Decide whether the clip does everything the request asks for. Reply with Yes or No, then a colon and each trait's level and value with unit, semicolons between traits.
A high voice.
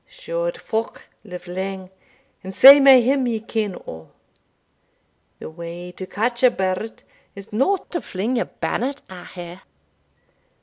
Yes: high, 215 Hz